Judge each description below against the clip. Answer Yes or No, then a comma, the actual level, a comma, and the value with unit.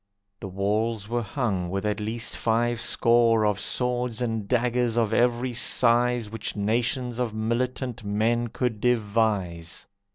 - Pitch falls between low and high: No, low, 115 Hz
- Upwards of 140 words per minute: No, slow, 135 wpm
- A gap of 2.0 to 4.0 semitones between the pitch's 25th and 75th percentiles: Yes, narrow, 2.5 semitones